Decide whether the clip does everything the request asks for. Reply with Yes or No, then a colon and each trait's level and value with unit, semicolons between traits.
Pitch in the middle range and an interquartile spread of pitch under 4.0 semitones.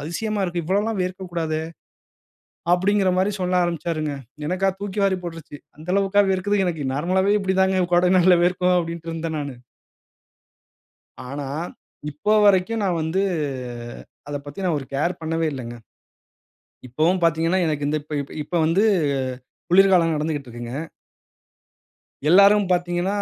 Yes: medium, 175 Hz; average, 3.3 semitones